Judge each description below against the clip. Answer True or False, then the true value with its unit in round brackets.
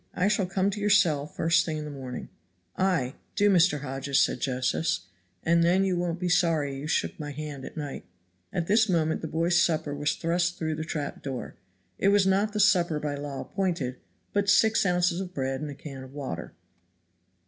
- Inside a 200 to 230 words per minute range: True (205 wpm)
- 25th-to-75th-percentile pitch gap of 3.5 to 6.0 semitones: True (4.4 semitones)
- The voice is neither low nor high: True (165 Hz)